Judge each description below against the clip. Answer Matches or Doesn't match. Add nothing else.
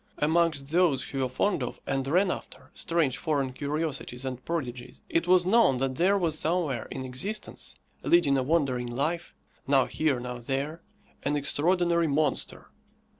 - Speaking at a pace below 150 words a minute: Doesn't match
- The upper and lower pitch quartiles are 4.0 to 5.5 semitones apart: Matches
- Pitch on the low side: Doesn't match